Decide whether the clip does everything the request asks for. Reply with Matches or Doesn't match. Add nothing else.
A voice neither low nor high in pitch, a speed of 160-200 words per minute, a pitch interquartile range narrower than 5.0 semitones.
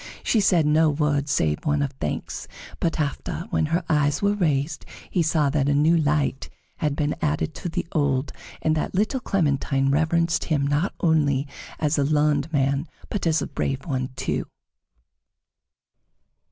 Matches